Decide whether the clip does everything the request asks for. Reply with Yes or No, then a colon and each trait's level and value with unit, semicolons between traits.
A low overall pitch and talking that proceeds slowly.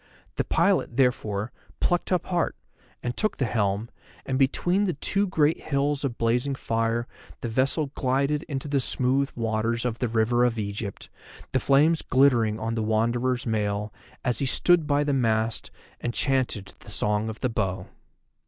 No: low, 125 Hz; average, 165 wpm